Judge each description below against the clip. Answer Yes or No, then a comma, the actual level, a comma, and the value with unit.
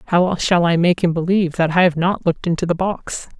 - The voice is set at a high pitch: No, medium, 175 Hz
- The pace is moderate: No, fast, 250 wpm